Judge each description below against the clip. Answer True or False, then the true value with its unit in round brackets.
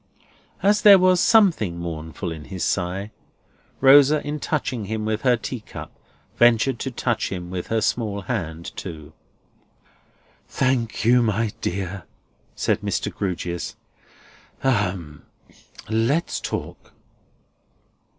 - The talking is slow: True (115 wpm)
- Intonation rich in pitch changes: True (6.3 semitones)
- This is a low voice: True (110 Hz)